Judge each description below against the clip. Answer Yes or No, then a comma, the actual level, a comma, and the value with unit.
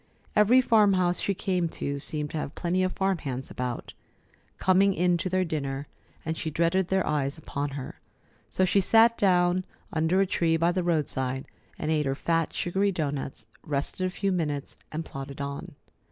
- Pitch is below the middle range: No, medium, 165 Hz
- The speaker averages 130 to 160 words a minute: No, average, 180 wpm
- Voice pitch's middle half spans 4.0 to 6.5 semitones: Yes, average, 4.5 semitones